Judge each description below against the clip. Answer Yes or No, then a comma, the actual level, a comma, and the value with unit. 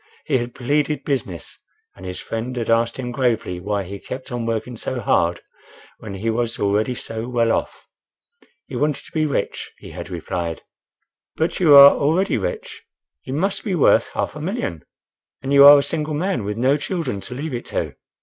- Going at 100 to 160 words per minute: No, average, 190 wpm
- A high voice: No, low, 125 Hz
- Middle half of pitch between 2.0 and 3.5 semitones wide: No, average, 4.9 semitones